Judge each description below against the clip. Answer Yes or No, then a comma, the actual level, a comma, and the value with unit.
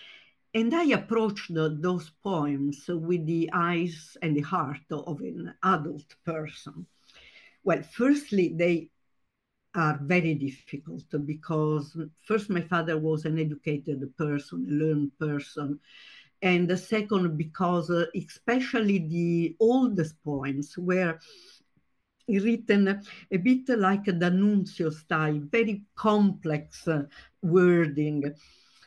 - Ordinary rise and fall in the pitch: Yes, average, 4.0 semitones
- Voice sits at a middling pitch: Yes, medium, 170 Hz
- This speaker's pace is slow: Yes, slow, 105 wpm